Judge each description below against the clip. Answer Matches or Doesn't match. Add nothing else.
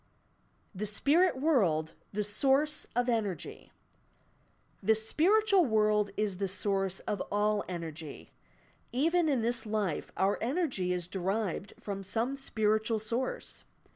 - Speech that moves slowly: Matches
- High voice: Matches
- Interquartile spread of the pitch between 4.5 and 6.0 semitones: Matches